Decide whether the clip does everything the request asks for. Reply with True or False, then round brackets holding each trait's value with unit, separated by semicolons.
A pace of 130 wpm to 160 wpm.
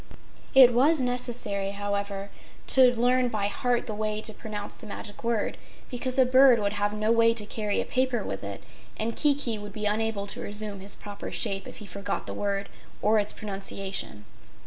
False (190 wpm)